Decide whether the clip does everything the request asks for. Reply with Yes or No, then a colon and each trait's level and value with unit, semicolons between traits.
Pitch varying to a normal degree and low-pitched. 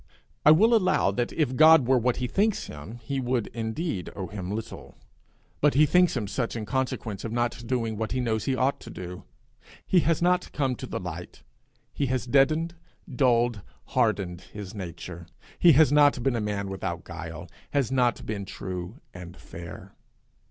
No: wide, 5.7 semitones; low, 120 Hz